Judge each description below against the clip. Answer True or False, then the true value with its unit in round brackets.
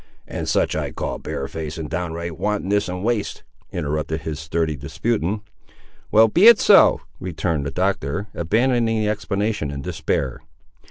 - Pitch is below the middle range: True (90 Hz)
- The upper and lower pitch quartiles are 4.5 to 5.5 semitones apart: True (5.2 semitones)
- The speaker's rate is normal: True (145 wpm)